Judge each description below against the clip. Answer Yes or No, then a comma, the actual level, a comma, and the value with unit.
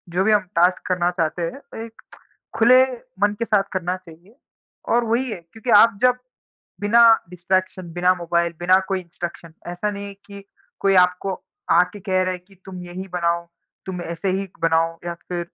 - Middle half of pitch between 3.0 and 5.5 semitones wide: No, narrow, 2.6 semitones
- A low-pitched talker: No, medium, 185 Hz